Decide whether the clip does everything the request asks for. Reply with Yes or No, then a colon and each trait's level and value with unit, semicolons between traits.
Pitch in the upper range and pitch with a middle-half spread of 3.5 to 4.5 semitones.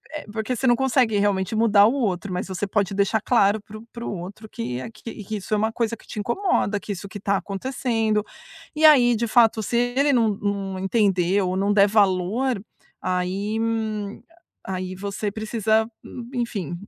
No: high, 210 Hz; average, 2.8 semitones